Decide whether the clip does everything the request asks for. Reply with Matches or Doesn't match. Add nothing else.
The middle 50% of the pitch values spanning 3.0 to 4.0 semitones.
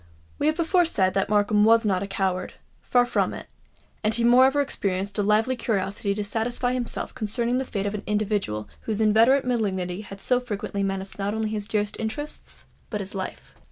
Matches